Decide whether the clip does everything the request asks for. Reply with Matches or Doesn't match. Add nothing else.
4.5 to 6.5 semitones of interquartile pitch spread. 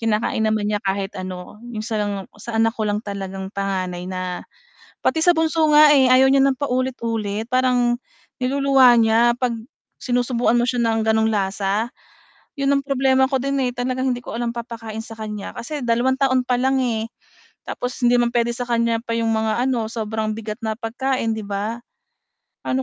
Doesn't match